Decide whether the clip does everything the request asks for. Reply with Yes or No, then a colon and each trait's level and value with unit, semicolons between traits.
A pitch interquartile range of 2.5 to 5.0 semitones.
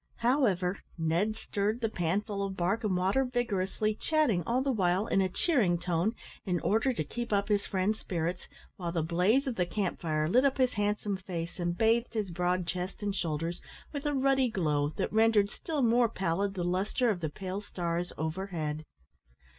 Yes: average, 4.3 semitones